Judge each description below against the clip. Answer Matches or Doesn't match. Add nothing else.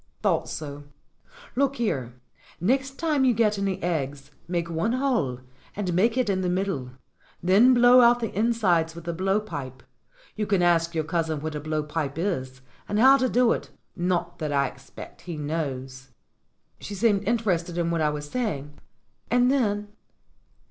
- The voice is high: Doesn't match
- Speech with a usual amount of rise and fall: Doesn't match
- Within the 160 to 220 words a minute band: Matches